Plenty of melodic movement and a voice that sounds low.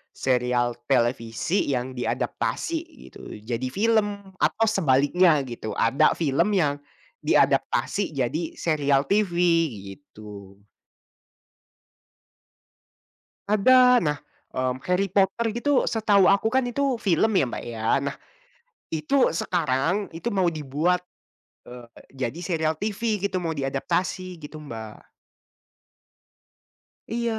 No: wide, 7.5 semitones; medium, 165 Hz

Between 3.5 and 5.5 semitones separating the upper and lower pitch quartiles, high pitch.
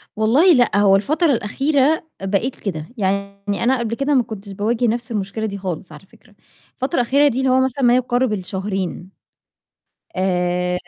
Yes: average, 4.9 semitones; high, 220 Hz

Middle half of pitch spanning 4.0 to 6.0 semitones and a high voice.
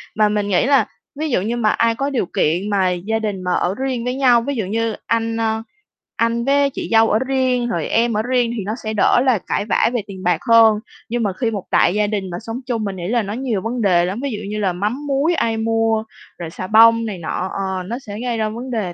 No: average, 3.1 semitones; high, 225 Hz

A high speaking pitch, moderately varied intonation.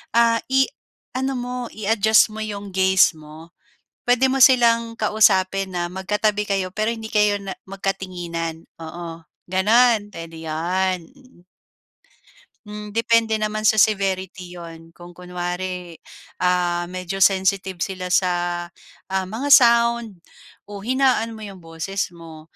Yes: high, 195 Hz; average, 3.6 semitones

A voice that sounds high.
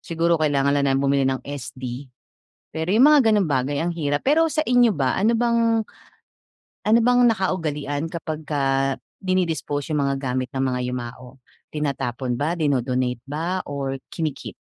No: medium, 145 Hz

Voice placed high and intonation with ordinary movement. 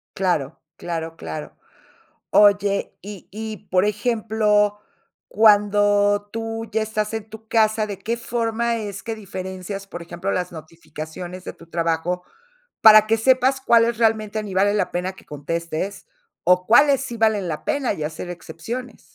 Yes: high, 205 Hz; average, 3.5 semitones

